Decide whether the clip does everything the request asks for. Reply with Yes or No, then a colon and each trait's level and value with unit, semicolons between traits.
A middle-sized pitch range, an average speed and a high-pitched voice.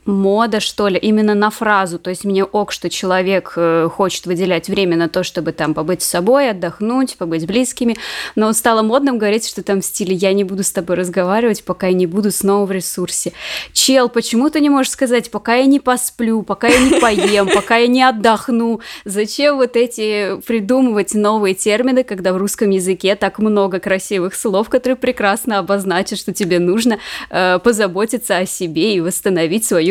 No: average, 3.7 semitones; fast, 185 wpm; high, 205 Hz